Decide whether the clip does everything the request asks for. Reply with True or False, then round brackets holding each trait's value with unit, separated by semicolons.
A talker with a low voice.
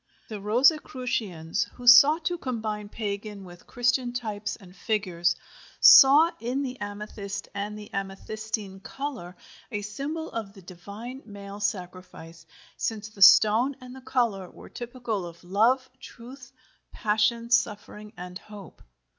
False (215 Hz)